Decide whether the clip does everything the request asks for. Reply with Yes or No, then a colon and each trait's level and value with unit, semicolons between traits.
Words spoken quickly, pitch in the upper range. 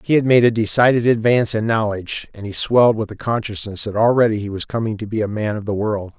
No: fast, 250 wpm; low, 110 Hz